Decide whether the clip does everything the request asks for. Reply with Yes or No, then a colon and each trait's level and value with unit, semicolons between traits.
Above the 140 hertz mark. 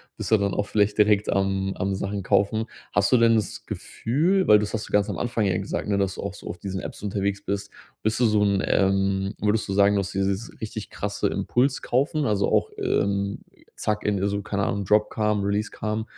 No: low, 100 Hz